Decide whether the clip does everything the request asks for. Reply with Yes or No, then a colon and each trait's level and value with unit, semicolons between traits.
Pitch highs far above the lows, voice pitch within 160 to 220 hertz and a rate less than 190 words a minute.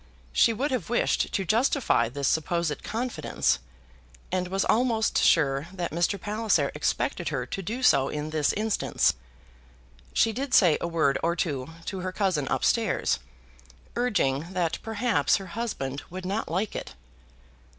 Yes: wide, 6.1 semitones; medium, 185 Hz; average, 150 wpm